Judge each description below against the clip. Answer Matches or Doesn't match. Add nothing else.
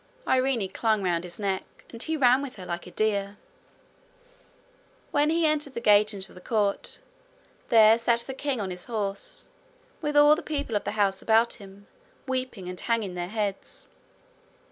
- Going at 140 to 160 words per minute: Doesn't match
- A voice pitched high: Matches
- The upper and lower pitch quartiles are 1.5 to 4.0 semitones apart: Doesn't match